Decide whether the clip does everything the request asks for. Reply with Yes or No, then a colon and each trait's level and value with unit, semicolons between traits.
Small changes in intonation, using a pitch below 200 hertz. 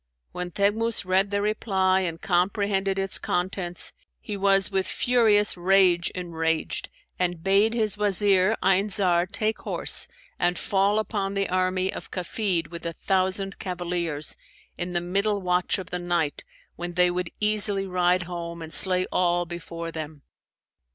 Yes: narrow, 2.1 semitones; medium, 185 Hz